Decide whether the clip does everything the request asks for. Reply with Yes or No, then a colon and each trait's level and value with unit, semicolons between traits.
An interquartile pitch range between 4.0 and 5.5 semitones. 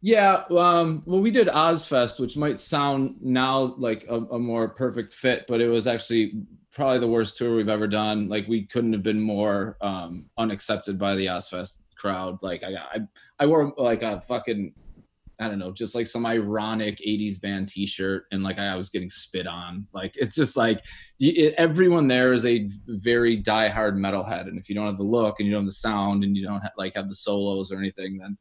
No: average, 3.6 semitones